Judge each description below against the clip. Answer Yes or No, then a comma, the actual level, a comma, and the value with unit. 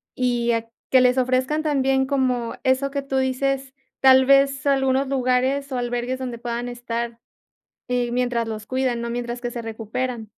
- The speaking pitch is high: Yes, very high, 255 Hz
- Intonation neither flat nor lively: No, narrow, 1.9 semitones